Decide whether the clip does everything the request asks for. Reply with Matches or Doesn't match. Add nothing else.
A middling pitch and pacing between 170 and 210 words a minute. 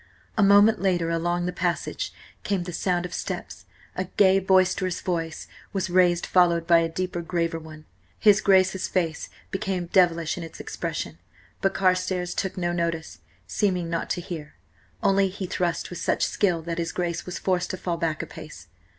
Matches